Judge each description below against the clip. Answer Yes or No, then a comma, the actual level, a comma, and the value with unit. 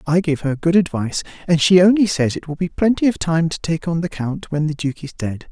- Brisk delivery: Yes, fast, 270 wpm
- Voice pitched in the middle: Yes, medium, 165 Hz